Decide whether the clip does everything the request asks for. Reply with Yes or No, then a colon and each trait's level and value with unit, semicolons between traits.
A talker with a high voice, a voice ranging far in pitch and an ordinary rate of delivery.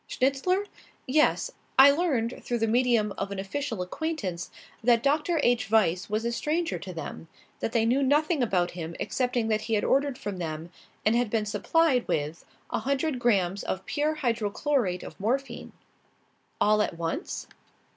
Yes: high, 235 Hz; wide, 5.8 semitones; average, 160 wpm